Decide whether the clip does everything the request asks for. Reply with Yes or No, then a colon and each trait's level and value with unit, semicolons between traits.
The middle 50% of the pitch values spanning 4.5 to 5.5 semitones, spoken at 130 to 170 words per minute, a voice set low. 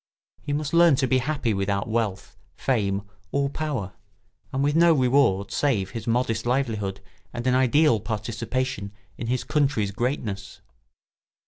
Yes: average, 5.0 semitones; average, 140 wpm; low, 120 Hz